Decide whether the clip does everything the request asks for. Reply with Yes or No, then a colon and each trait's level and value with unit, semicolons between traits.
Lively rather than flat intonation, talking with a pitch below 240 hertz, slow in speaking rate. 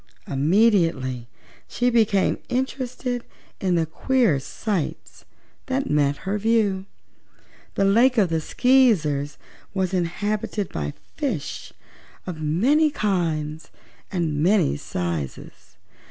Yes: wide, 7.0 semitones; high, 190 Hz; slow, 100 wpm